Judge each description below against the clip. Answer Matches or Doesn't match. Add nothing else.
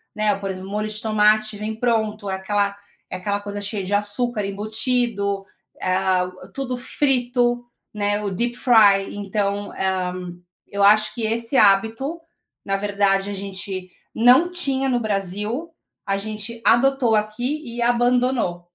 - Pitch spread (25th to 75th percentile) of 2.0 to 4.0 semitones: Matches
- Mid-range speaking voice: Doesn't match